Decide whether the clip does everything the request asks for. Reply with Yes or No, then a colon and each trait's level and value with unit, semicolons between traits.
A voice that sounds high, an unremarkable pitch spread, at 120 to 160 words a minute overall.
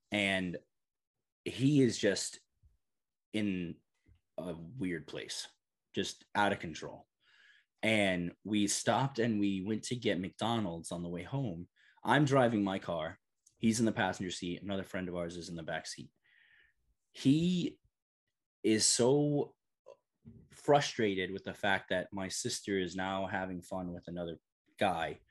No: very low, 95 Hz; average, 3.7 semitones; average, 140 wpm